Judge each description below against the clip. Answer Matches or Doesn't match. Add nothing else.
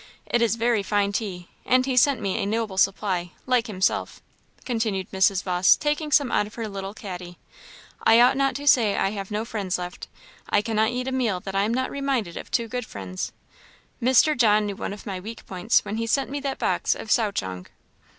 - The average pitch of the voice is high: Matches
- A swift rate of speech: Matches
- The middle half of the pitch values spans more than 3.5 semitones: Matches